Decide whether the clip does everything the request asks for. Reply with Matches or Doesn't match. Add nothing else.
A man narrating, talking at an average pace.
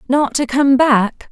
Doesn't match